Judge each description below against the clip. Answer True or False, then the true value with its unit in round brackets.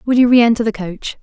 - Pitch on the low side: False (225 Hz)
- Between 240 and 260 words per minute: True (245 wpm)